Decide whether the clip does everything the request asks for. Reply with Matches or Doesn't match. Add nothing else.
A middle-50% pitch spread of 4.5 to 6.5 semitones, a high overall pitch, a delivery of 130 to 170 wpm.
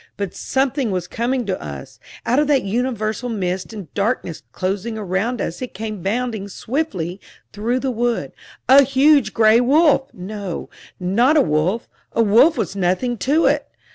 Matches